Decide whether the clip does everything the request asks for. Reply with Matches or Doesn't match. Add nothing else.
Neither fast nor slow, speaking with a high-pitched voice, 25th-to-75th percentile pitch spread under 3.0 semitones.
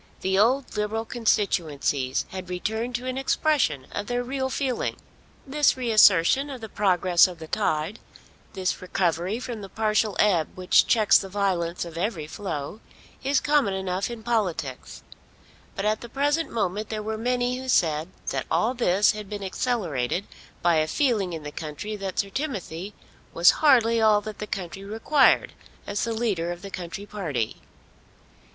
Doesn't match